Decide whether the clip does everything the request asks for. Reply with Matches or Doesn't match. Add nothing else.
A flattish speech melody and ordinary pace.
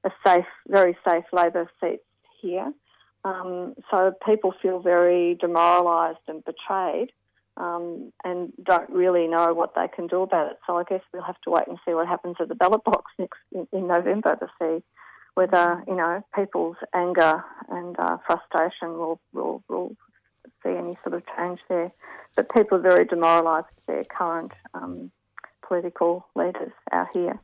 Matches